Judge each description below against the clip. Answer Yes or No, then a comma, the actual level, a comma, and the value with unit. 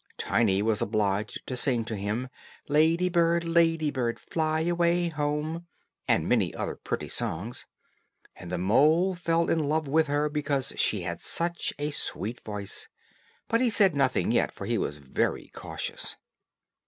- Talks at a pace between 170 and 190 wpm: No, average, 155 wpm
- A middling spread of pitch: No, wide, 6.9 semitones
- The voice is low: No, medium, 150 Hz